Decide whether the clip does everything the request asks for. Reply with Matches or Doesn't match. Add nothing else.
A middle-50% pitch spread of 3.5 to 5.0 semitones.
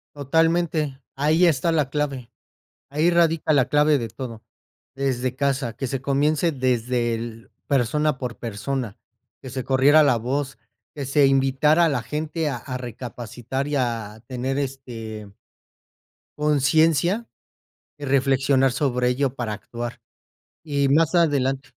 Doesn't match